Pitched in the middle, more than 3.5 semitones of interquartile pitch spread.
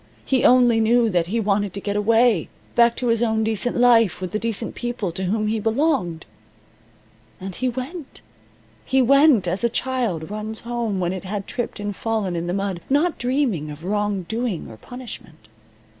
No: high, 220 Hz; average, 4.0 semitones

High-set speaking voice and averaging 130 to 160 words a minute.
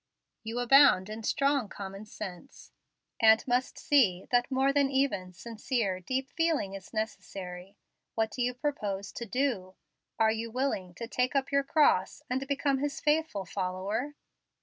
Yes: high, 235 Hz; average, 150 wpm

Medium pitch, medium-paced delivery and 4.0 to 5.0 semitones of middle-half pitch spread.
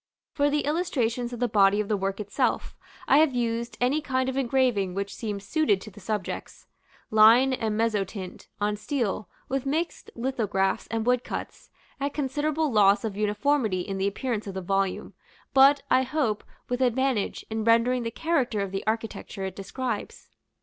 No: high, 230 Hz; average, 170 wpm; average, 4.4 semitones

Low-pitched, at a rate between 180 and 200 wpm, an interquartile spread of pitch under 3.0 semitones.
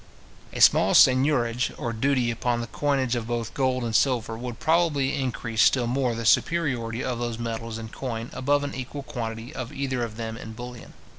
Yes: low, 120 Hz; average, 190 wpm; narrow, 2.5 semitones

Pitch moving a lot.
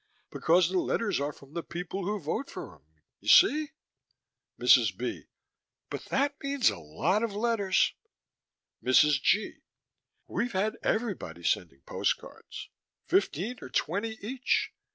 Yes: wide, 7.5 semitones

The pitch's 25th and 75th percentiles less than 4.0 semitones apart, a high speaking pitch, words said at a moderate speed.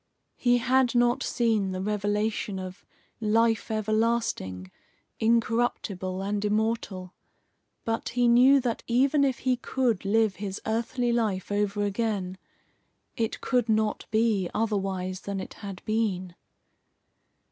No: average, 3.1 semitones; high, 215 Hz; slow, 120 wpm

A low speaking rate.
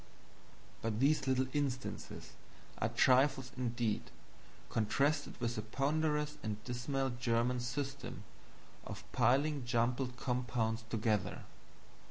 Yes: slow, 100 wpm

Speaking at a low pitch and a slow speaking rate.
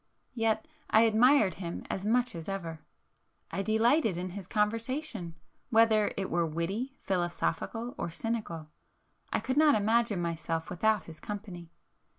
No: high, 210 Hz; slow, 130 wpm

